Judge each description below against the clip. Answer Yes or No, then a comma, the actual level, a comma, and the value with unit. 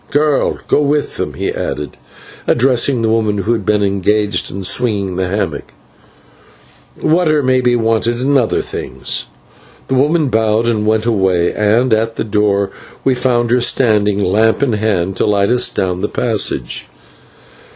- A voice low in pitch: Yes, low, 110 Hz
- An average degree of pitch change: Yes, average, 3.6 semitones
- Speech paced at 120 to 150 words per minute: No, average, 160 wpm